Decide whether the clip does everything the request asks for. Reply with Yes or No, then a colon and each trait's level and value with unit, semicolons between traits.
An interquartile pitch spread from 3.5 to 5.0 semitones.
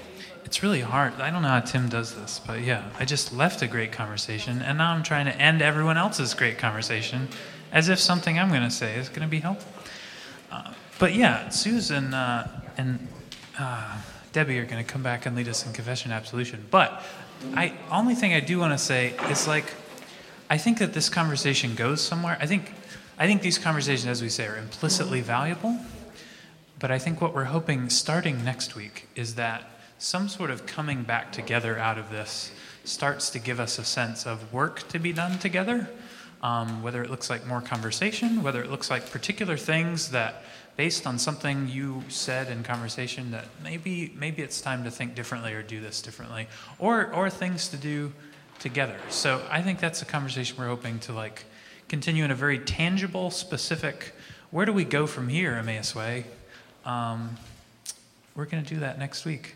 No: wide, 5.4 semitones